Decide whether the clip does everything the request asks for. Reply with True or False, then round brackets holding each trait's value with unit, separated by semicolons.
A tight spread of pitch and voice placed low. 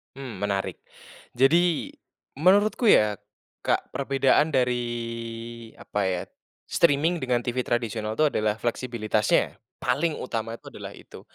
False (3.9 semitones; 120 Hz)